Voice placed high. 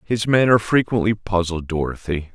No: low, 100 Hz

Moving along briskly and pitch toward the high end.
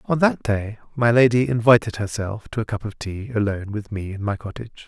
No: fast, 220 wpm; low, 110 Hz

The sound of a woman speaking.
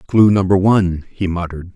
No: male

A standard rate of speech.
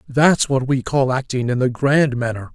No: fast, 210 wpm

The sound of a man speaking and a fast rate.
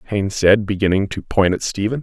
Yes: male; fast, 210 wpm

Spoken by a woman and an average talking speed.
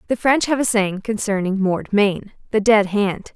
Yes: female; average, 180 wpm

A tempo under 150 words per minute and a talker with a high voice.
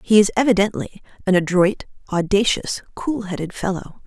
Yes: slow, 135 wpm; high, 195 Hz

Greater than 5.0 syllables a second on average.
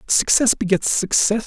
No: 4.5 syllables/s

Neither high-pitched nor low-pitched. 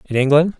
Yes: medium, 150 Hz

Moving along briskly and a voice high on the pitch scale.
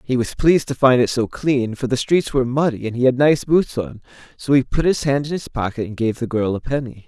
No: fast, 280 wpm; low, 130 Hz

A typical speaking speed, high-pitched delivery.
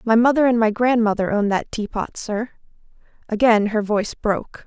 Yes: average, 165 wpm; high, 220 Hz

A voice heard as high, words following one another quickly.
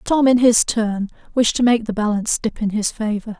Yes: high, 225 Hz; fast, 230 wpm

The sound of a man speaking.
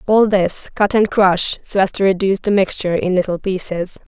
No: female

